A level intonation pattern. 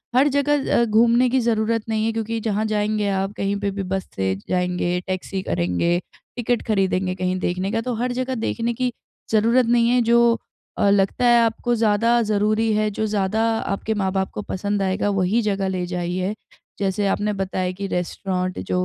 No: average, 3.4 semitones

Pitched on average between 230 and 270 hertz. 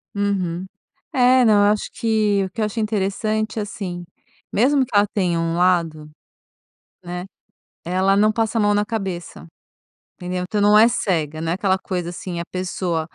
No: high, 195 Hz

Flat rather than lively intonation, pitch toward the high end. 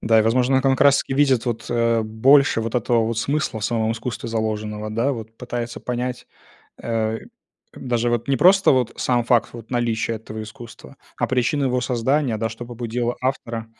No: narrow, 2.2 semitones; low, 120 Hz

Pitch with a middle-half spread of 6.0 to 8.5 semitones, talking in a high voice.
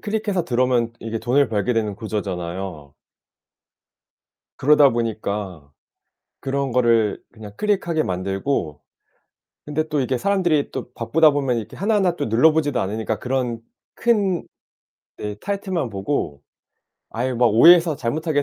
No: wide, 6.6 semitones; low, 125 Hz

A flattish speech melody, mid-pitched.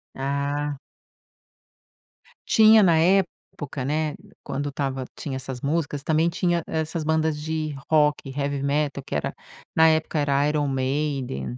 Yes: narrow, 2.3 semitones; medium, 145 Hz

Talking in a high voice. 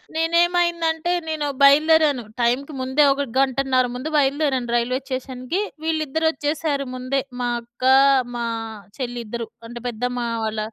Yes: very high, 275 Hz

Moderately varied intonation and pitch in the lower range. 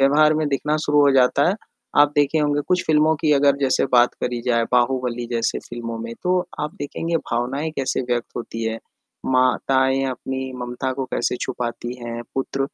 Yes: average, 3.2 semitones; low, 130 Hz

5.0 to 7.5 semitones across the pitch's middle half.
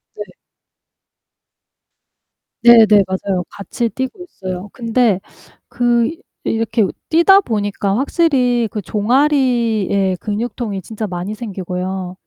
No: average, 3.9 semitones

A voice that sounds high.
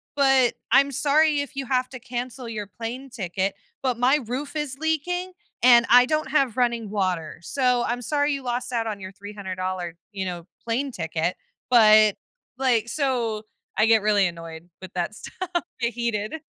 Yes: high, 235 Hz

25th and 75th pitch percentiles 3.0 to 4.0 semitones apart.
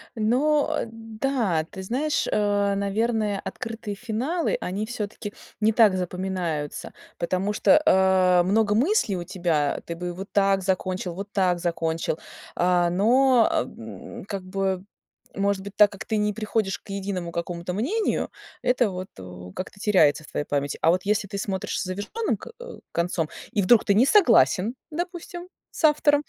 Yes: average, 3.6 semitones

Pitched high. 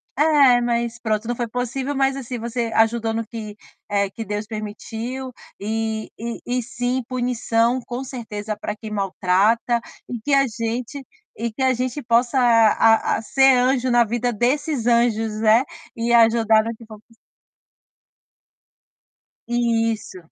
Yes: high, 235 Hz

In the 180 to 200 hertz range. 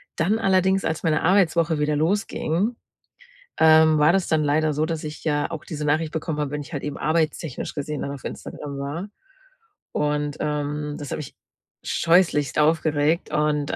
No: medium, 155 Hz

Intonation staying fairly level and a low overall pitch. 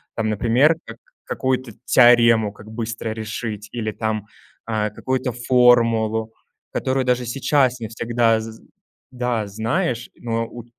Yes: narrow, 1.9 semitones; low, 115 Hz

